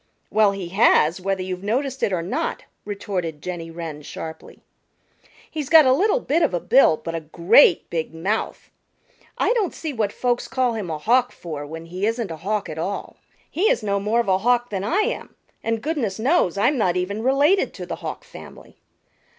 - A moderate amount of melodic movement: No, wide, 6.6 semitones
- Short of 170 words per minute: No, average, 200 wpm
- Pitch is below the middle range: No, high, 205 Hz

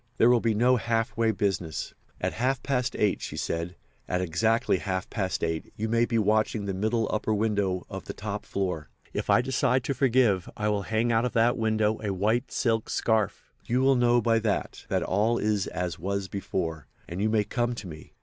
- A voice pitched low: Yes, low, 110 Hz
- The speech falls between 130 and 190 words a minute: No, fast, 205 wpm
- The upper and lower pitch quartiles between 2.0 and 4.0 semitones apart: Yes, average, 3.3 semitones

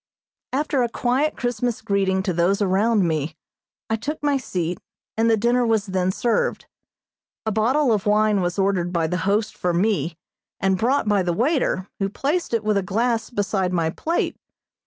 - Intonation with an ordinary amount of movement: Yes, average, 4.3 semitones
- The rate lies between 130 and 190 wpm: Yes, average, 180 wpm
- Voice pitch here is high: Yes, high, 210 Hz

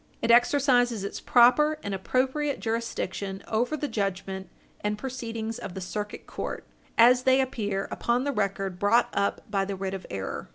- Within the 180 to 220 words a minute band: No, average, 165 wpm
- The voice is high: Yes, high, 225 Hz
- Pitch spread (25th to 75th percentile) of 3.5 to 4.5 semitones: Yes, average, 4.2 semitones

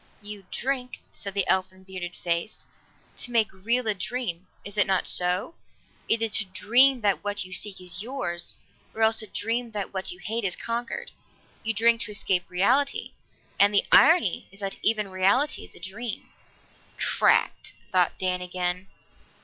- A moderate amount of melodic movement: Yes, average, 3.7 semitones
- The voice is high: Yes, high, 205 Hz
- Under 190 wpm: Yes, average, 165 wpm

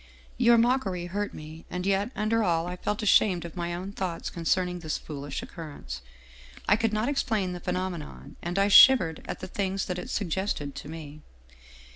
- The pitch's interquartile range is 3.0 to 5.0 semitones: Yes, average, 3.7 semitones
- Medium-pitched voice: Yes, medium, 180 Hz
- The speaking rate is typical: Yes, average, 180 wpm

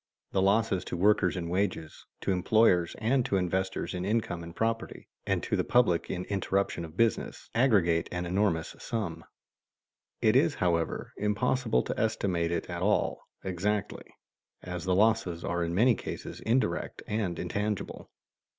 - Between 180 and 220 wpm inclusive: No, average, 155 wpm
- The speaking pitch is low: Yes, very low, 95 Hz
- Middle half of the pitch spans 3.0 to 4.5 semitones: Yes, average, 3.7 semitones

